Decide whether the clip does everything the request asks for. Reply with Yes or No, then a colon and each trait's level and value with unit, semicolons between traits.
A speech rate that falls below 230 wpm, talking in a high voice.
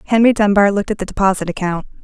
Yes: fast, 205 wpm; high, 200 Hz